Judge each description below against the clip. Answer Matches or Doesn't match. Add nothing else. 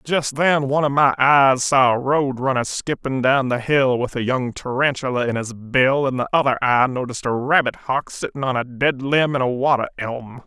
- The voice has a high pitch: Doesn't match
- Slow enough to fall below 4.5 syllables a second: Doesn't match